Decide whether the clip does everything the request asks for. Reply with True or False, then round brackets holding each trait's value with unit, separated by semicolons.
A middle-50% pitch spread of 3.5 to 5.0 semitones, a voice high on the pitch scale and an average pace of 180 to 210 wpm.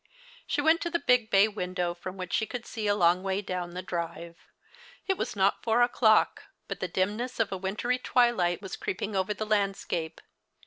True (4.1 semitones; 200 Hz; 195 wpm)